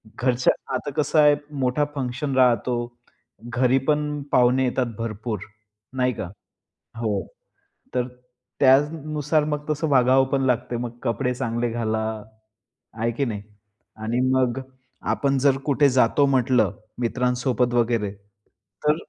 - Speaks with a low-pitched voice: Yes, low, 125 Hz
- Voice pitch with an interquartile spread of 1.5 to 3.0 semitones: Yes, average, 2.7 semitones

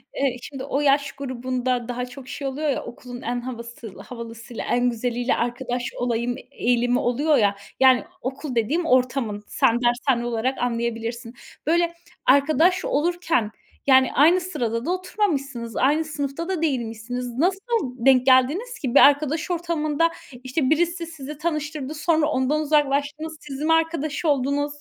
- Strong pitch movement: No, average, 4.0 semitones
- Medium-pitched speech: No, very high, 270 Hz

